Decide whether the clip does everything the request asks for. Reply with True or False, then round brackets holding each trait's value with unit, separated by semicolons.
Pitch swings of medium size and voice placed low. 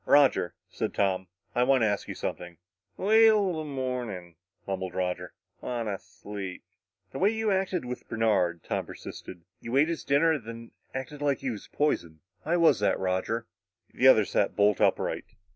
False (7.7 semitones; 115 Hz)